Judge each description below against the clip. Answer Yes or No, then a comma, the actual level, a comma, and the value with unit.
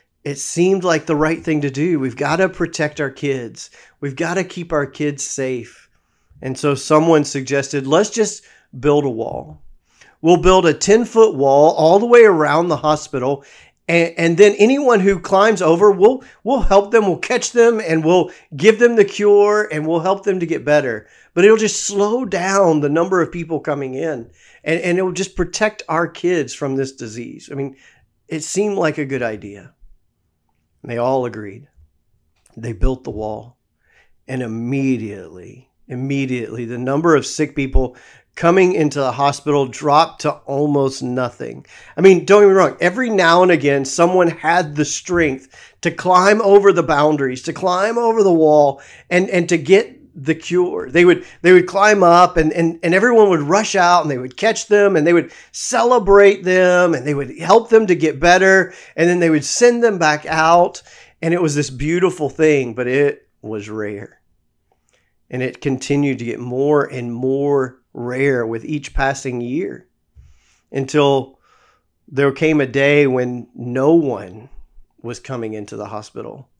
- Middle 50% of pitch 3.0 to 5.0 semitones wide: No, wide, 5.4 semitones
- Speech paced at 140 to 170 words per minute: No, average, 180 wpm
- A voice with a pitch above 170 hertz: No, medium, 155 Hz